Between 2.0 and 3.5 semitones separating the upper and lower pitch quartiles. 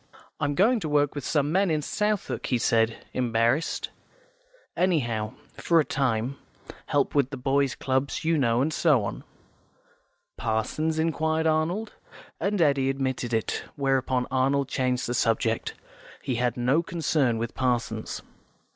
No: average, 4.4 semitones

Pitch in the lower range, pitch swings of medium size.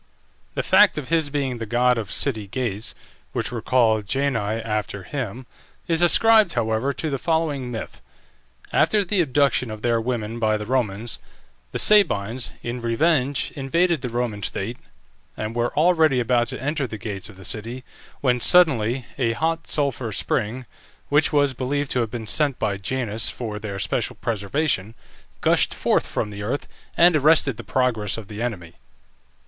Yes: low, 125 Hz; average, 4.6 semitones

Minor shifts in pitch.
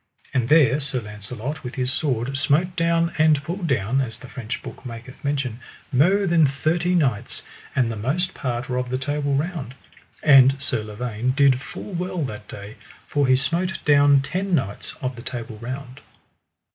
No: average, 3.8 semitones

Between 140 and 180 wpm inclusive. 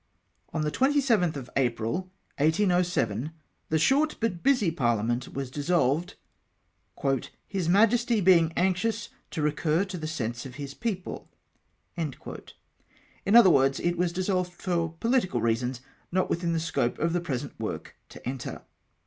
Yes: average, 145 wpm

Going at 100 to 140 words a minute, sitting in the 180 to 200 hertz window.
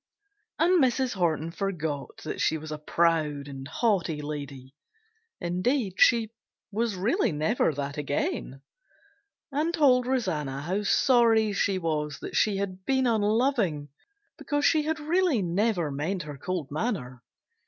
Yes: slow, 135 wpm; medium, 185 Hz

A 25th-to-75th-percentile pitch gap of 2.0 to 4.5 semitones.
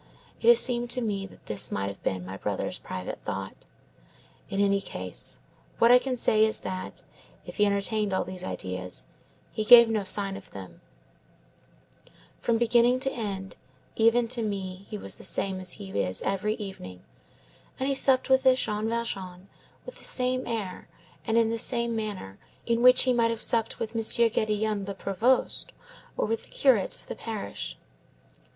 Yes: average, 3.8 semitones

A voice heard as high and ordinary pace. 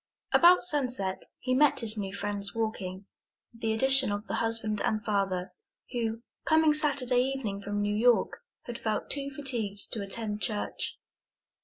Yes: high, 225 Hz; average, 155 wpm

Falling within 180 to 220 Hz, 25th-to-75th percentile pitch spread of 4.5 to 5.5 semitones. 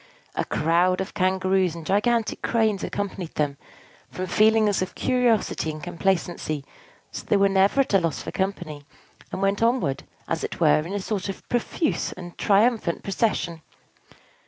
No: high, 190 Hz; average, 3.7 semitones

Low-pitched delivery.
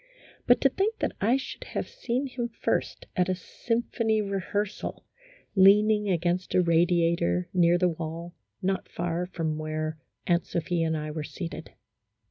No: medium, 180 Hz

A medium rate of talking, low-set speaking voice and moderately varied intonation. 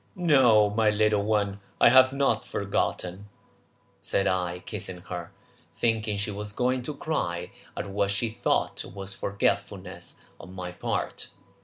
Yes: average, 145 wpm; low, 105 Hz; average, 3.1 semitones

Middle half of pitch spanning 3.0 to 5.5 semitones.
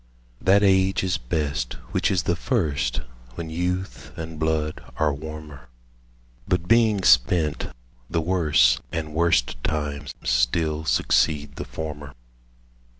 Yes: average, 3.4 semitones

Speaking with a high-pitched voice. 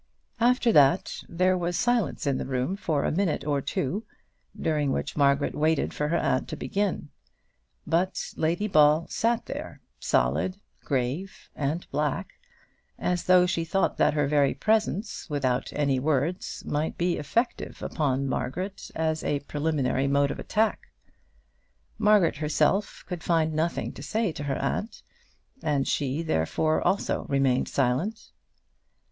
No: medium, 155 Hz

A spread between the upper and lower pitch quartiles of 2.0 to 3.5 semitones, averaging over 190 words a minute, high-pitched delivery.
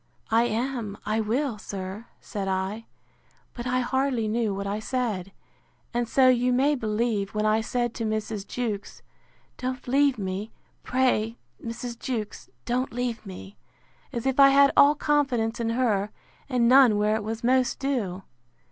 No: average, 3.1 semitones; average, 155 wpm; high, 230 Hz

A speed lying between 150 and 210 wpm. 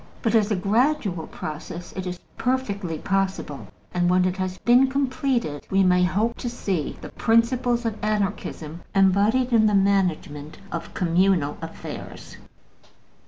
No: average, 140 wpm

